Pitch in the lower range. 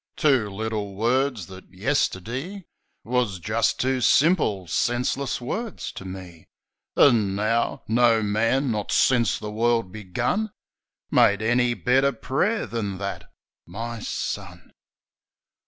Yes: low, 115 Hz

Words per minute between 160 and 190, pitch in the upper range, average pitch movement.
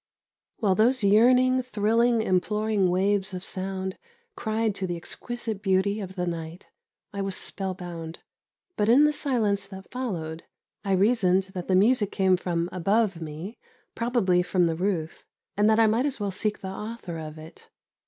Yes: average, 165 wpm; high, 195 Hz; average, 3.3 semitones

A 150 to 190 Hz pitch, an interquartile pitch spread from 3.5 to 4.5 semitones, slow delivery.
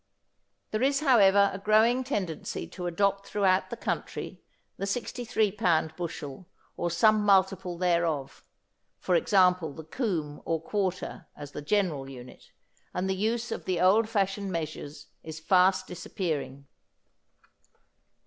Yes: medium, 185 Hz; average, 4.2 semitones; slow, 130 wpm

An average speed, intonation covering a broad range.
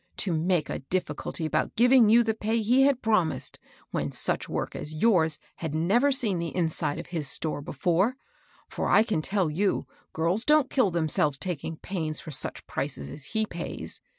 Yes: average, 185 wpm; wide, 5.9 semitones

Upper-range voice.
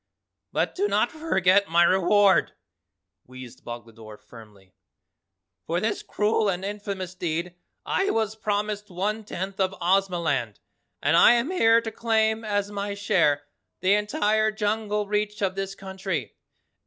Yes: high, 200 Hz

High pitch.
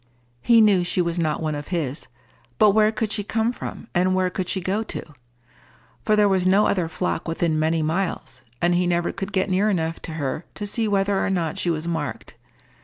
No: medium, 180 Hz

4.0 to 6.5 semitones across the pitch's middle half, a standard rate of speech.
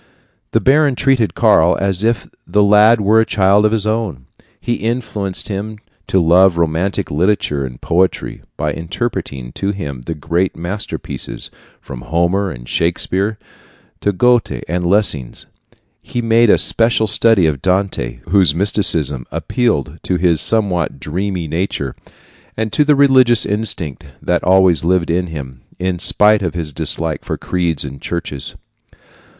Yes: average, 4.7 semitones; average, 145 wpm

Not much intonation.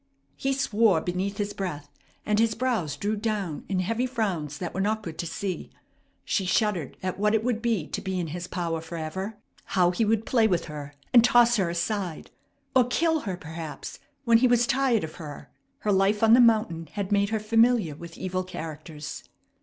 No: average, 4.8 semitones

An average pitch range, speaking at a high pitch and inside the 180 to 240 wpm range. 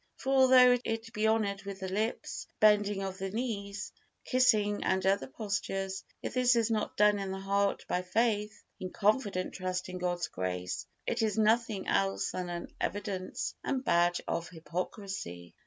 No: average, 3.0 semitones; high, 200 Hz; average, 165 wpm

